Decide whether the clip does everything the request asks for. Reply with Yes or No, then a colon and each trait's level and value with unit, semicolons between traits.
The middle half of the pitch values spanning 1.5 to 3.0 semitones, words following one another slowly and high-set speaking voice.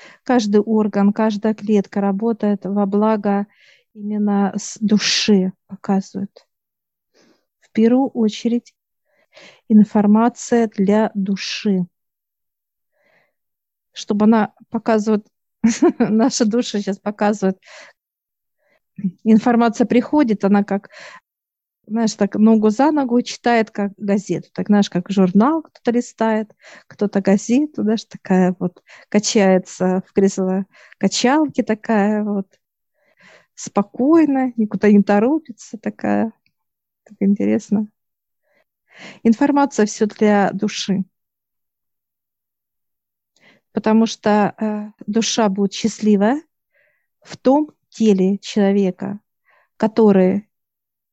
Yes: narrow, 2.4 semitones; slow, 85 wpm; high, 210 Hz